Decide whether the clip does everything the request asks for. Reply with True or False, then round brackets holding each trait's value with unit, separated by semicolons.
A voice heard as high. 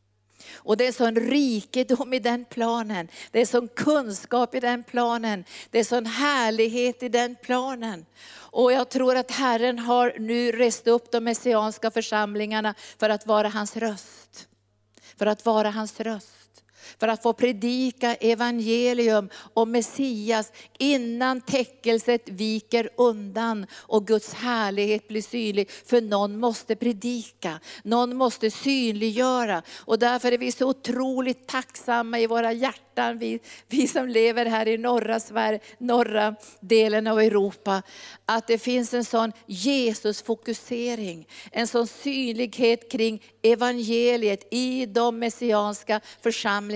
True (230 Hz)